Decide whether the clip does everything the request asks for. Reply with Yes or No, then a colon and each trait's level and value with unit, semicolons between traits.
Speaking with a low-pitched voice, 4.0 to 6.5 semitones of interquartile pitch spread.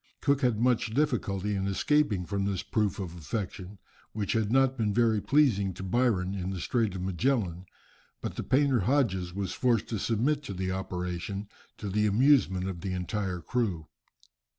Yes: low, 100 Hz; average, 4.5 semitones